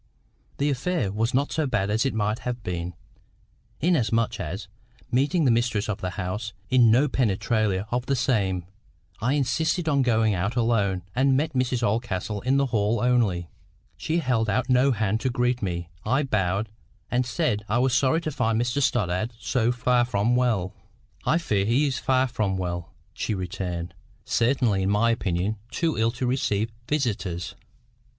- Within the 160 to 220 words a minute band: Yes, average, 170 wpm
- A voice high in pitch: No, low, 115 Hz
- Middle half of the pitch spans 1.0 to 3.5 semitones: No, average, 4.2 semitones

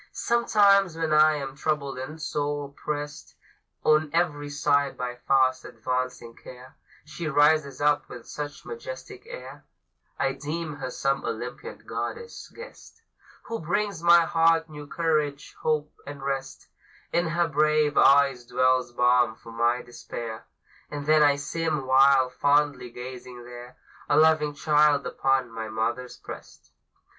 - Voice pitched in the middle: Yes, medium, 145 Hz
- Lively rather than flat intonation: No, average, 3.2 semitones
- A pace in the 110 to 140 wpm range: Yes, slow, 135 wpm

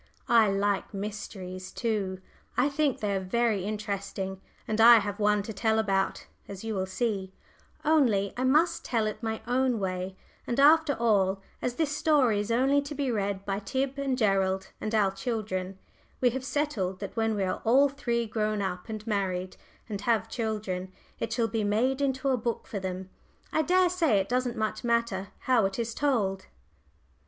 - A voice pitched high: Yes, high, 220 Hz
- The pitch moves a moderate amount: Yes, average, 4.2 semitones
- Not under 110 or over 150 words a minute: No, average, 180 wpm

